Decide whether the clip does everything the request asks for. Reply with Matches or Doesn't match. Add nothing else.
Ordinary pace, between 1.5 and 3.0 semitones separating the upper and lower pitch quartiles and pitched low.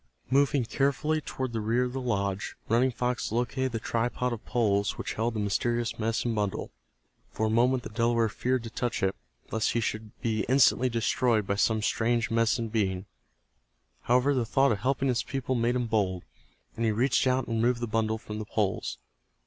Matches